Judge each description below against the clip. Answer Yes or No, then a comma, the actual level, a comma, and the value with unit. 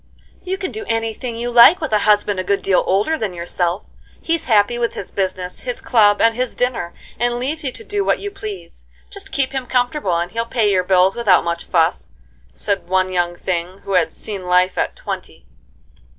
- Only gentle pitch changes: No, average, 5.1 semitones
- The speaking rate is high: Yes, fast, 210 wpm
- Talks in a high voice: Yes, high, 205 Hz